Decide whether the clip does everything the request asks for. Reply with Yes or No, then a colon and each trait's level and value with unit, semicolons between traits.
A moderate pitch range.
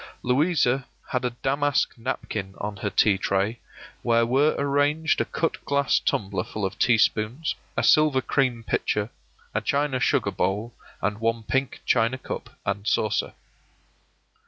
Yes: average, 4.8 semitones